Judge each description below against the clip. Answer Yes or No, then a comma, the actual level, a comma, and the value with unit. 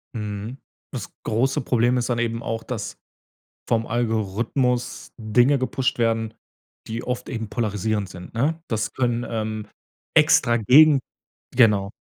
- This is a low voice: Yes, low, 115 Hz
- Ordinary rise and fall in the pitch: No, narrow, 2.3 semitones